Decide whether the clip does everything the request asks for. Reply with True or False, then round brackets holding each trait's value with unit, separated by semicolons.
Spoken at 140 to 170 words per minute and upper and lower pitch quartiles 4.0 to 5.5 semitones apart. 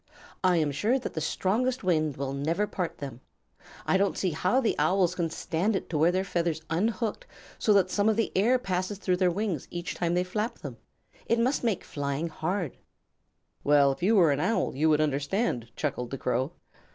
False (200 wpm; 5.1 semitones)